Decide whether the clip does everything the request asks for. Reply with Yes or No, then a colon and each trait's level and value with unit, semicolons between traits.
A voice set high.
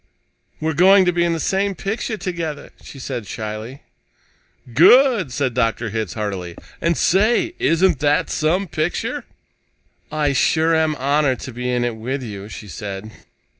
No: medium, 145 Hz